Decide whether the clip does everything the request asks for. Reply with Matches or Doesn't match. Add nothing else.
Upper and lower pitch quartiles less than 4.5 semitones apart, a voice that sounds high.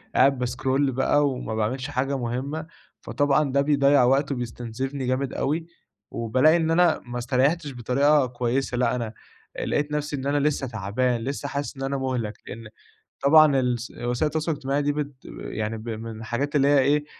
Doesn't match